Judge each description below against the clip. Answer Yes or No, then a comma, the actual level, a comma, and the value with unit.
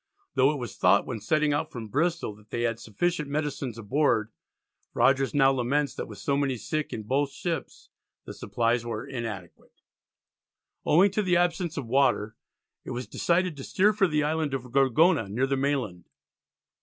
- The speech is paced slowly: No, average, 175 wpm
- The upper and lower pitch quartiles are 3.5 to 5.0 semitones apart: Yes, average, 4.7 semitones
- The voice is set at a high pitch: No, low, 135 Hz